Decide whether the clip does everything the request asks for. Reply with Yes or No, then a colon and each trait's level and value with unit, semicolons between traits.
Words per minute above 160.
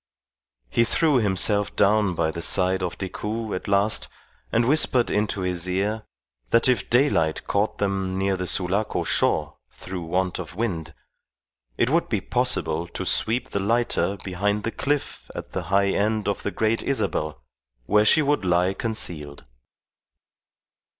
No: average, 150 wpm